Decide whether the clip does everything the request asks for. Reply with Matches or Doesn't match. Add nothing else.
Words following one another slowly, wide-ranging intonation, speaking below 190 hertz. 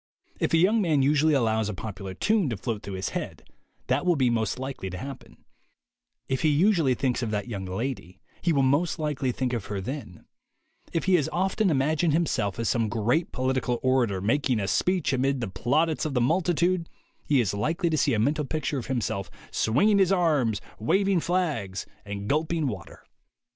Doesn't match